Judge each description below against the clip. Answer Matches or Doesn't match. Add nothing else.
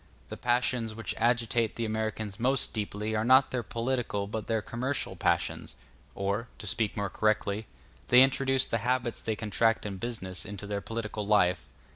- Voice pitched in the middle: Doesn't match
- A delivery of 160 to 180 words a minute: Matches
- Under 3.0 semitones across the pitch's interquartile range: Matches